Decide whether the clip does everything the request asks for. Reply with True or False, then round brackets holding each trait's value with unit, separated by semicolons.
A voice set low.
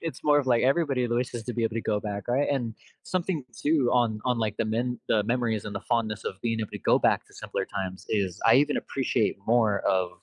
True (115 Hz)